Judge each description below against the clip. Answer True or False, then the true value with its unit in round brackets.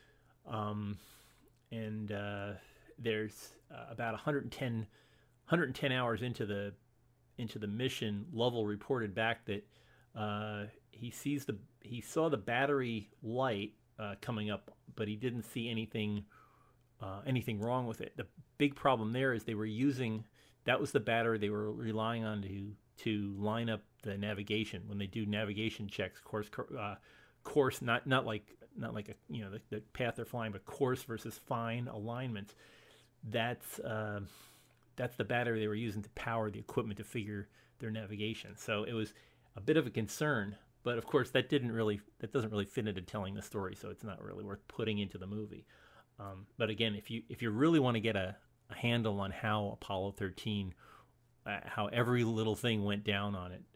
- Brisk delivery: False (180 wpm)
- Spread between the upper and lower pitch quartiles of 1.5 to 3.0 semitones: True (2.5 semitones)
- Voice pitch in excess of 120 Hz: False (110 Hz)